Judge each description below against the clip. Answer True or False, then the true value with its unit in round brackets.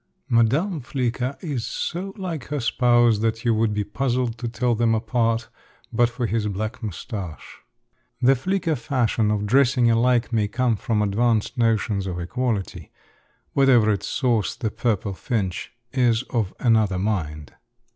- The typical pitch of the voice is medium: False (115 Hz)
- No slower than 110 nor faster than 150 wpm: True (145 wpm)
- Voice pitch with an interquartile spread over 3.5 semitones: False (2.9 semitones)